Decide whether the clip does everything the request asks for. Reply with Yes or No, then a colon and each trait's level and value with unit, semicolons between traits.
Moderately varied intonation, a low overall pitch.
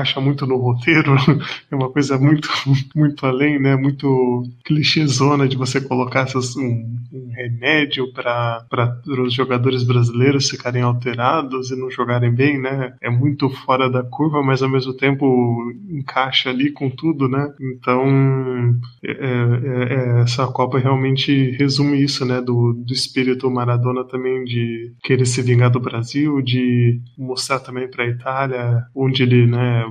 No: narrow, 1.8 semitones; low, 130 Hz